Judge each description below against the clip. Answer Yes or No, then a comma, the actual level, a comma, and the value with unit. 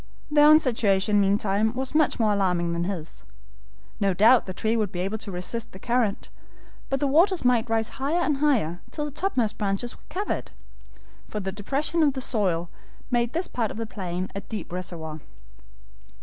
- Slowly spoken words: No, average, 185 wpm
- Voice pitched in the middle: No, high, 220 Hz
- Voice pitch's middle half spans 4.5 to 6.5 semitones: Yes, wide, 5.6 semitones